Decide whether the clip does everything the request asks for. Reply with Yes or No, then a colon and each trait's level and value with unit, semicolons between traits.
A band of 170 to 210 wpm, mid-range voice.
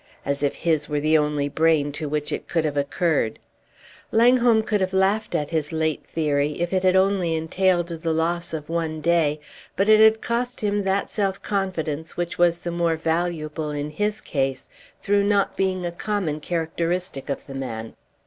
Yes: average, 185 wpm; medium, 165 Hz